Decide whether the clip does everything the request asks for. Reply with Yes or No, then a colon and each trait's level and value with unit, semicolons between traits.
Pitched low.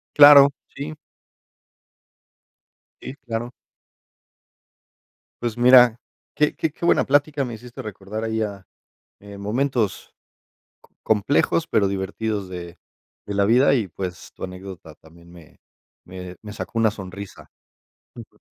Yes: low, 110 Hz